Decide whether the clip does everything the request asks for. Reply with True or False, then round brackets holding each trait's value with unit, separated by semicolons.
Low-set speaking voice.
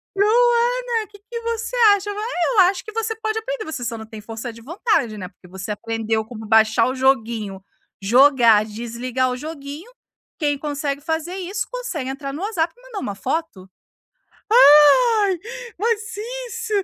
False (295 Hz)